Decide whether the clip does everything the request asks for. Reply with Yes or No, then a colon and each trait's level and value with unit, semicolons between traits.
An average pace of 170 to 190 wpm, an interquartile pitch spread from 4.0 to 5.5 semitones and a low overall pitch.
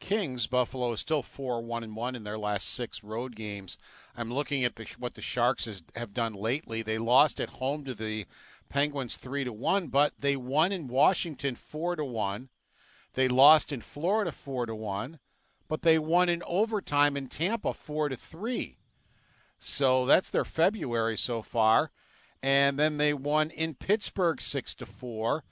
Yes: average, 175 wpm; average, 4.6 semitones; low, 130 Hz